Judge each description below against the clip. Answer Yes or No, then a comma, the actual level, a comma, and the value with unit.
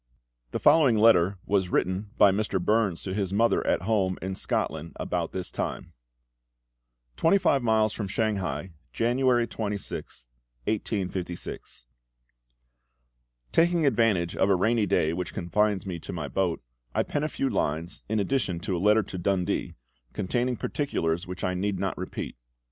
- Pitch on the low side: Yes, low, 100 Hz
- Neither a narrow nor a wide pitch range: Yes, average, 3.8 semitones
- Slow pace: No, average, 150 wpm